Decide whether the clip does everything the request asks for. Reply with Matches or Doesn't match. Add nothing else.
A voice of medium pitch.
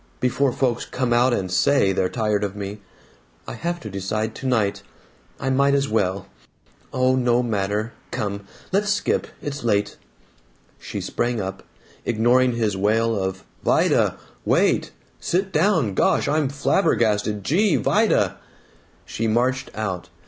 Doesn't match